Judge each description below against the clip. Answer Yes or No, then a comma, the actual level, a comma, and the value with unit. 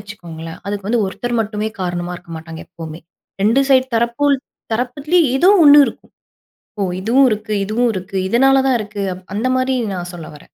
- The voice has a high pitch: Yes, high, 215 Hz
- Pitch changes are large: Yes, wide, 6.1 semitones